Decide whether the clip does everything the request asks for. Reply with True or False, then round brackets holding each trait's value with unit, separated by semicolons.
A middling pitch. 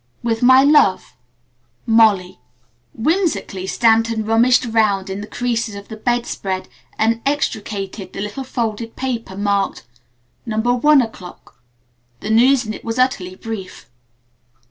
False (225 Hz)